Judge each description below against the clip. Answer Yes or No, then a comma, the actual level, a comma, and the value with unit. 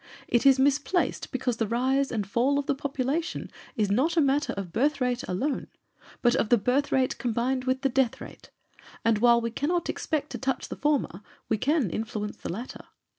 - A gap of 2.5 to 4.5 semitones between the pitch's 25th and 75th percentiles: Yes, average, 3.3 semitones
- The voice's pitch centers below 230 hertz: No, very high, 255 Hz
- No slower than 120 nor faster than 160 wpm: No, average, 195 wpm